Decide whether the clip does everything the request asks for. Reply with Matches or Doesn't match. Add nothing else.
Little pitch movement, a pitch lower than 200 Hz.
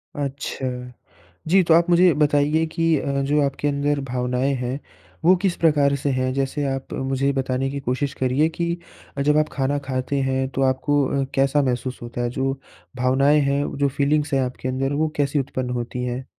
Matches